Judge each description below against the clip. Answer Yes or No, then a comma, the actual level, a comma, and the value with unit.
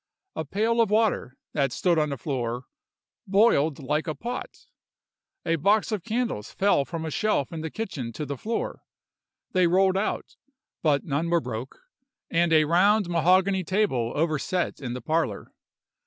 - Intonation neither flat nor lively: No, wide, 5.8 semitones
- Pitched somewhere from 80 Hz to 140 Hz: No, medium, 165 Hz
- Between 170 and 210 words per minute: No, average, 160 wpm